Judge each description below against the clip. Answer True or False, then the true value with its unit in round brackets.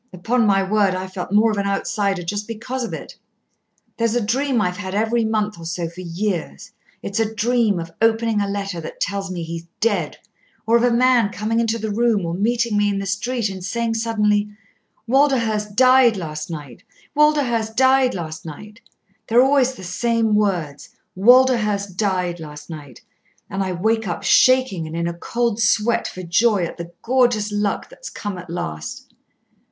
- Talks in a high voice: True (210 Hz)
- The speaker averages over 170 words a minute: True (180 wpm)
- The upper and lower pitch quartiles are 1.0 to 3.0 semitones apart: False (4.2 semitones)